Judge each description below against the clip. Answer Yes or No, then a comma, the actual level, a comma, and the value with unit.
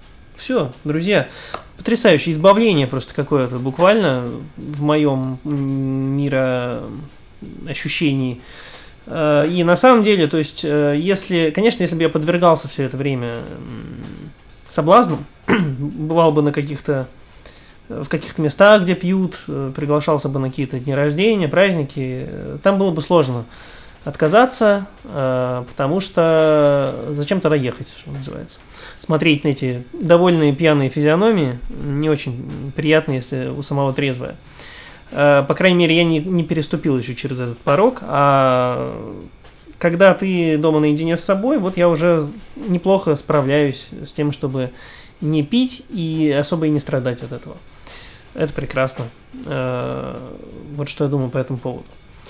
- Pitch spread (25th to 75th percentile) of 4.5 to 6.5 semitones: No, average, 4.0 semitones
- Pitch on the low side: No, medium, 150 Hz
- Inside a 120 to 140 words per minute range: Yes, average, 125 wpm